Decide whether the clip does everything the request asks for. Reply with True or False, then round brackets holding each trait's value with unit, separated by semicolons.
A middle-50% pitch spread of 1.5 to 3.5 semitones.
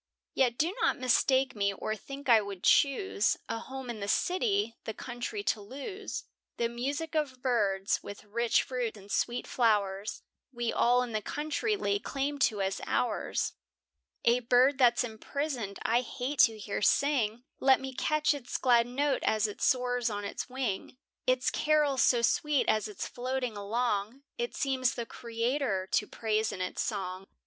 False (3.9 semitones)